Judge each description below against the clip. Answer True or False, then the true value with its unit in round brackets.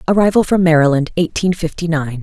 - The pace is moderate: True (160 wpm)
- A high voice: False (165 Hz)